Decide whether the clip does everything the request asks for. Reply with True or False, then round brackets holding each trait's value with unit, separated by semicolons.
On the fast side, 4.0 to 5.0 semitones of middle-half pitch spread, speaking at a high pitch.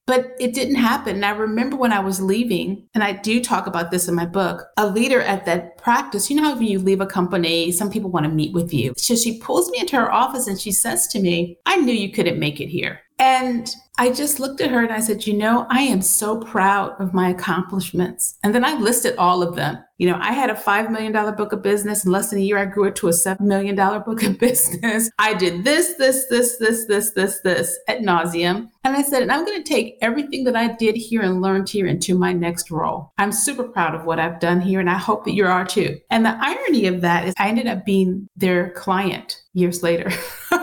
True (250 wpm; 4.4 semitones; 205 Hz)